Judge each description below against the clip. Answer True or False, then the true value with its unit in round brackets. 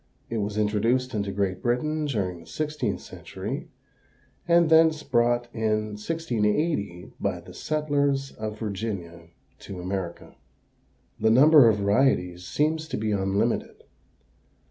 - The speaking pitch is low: True (110 Hz)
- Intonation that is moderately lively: False (6.3 semitones)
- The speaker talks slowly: True (120 wpm)